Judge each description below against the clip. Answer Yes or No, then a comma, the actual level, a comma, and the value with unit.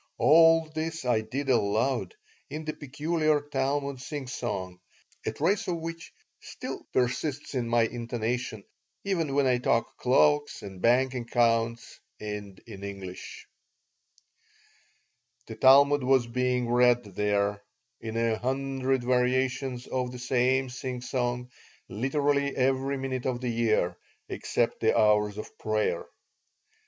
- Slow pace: Yes, slow, 125 wpm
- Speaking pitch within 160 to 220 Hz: No, low, 125 Hz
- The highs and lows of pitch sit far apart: No, average, 3.0 semitones